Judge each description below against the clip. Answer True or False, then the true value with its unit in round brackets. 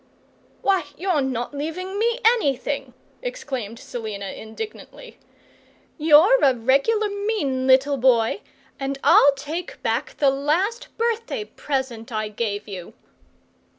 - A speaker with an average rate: False (115 wpm)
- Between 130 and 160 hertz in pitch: False (280 Hz)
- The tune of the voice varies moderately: False (8.5 semitones)